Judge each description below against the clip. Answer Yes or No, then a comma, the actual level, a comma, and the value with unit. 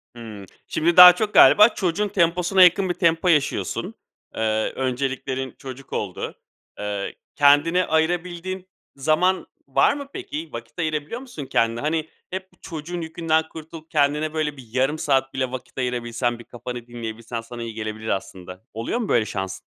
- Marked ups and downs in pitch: Yes, wide, 6.6 semitones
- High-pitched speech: No, medium, 150 Hz